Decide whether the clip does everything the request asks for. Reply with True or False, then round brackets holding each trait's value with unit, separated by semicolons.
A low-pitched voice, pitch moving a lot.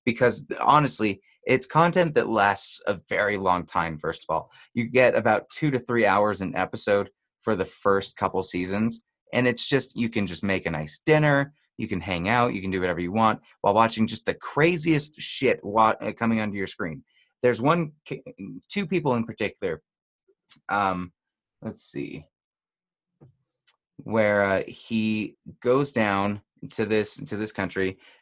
True (110 Hz; 5.7 semitones)